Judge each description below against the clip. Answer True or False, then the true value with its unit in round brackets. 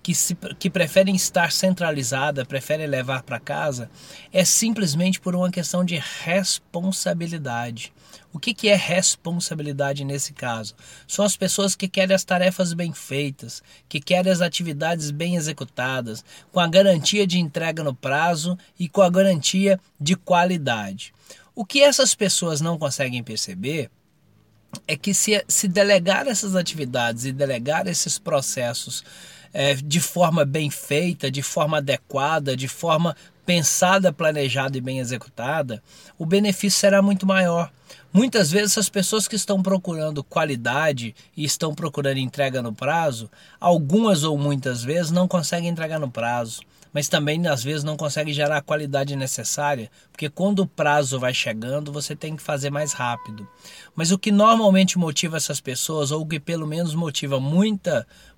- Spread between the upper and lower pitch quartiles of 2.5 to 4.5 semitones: False (5.0 semitones)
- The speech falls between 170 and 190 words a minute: False (150 wpm)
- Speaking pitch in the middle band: True (160 Hz)